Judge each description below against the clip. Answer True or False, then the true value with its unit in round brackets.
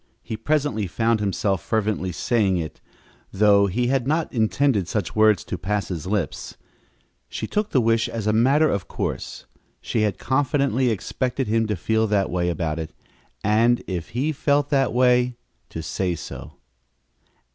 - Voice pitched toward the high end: False (110 Hz)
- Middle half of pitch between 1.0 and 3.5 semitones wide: False (4.4 semitones)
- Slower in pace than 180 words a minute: True (160 wpm)